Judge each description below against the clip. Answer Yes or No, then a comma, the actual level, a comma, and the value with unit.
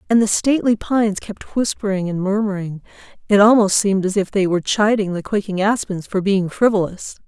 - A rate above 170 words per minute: Yes, average, 180 wpm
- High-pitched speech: Yes, high, 200 Hz